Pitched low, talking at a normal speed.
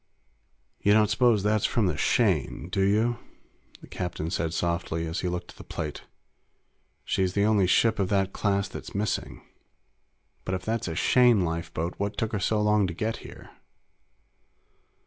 Yes: low, 100 Hz; average, 165 wpm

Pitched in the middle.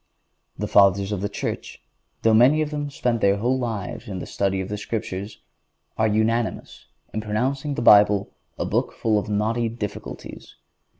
No: low, 110 Hz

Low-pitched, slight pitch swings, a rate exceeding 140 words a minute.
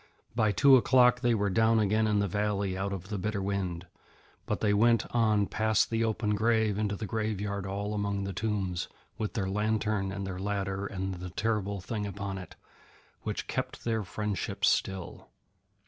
Yes: low, 105 Hz; narrow, 2.0 semitones; average, 180 wpm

